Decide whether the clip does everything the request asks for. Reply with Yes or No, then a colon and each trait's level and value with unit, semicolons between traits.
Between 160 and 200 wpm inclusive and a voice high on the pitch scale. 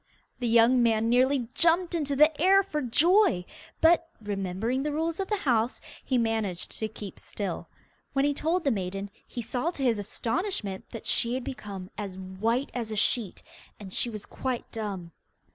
Yes: average, 180 wpm; high, 235 Hz